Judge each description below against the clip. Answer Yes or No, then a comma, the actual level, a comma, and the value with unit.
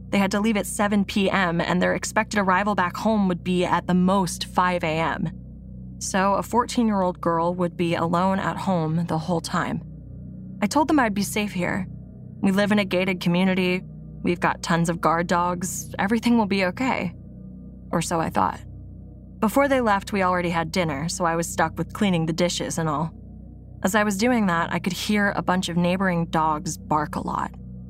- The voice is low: No, medium, 180 Hz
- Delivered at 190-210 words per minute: Yes, average, 200 wpm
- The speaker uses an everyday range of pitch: Yes, average, 3.3 semitones